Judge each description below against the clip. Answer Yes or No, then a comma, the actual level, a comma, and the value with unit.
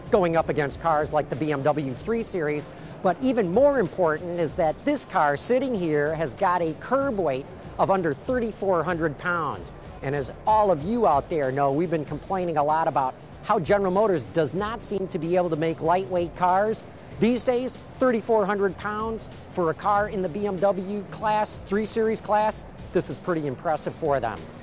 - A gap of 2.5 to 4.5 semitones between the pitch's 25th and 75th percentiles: No, wide, 5.5 semitones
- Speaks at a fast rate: No, average, 185 wpm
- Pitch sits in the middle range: Yes, medium, 180 Hz